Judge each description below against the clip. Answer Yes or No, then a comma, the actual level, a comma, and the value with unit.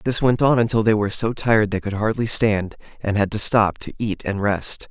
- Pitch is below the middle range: Yes, low, 110 Hz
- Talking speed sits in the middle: No, fast, 245 wpm